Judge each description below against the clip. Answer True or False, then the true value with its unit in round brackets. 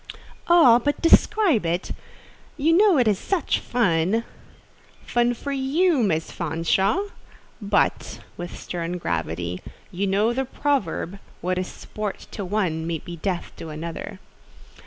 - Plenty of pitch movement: True (7.8 semitones)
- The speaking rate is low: True (125 wpm)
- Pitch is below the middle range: False (200 Hz)